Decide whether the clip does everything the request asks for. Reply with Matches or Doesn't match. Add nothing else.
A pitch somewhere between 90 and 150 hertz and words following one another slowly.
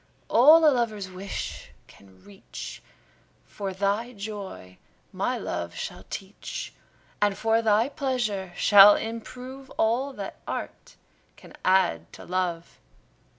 Doesn't match